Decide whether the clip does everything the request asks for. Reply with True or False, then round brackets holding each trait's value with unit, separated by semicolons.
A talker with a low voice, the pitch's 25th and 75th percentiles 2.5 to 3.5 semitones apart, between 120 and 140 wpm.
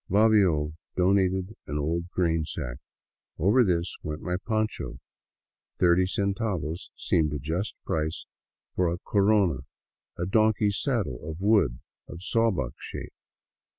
False (90 Hz; 4.3 semitones; 135 wpm)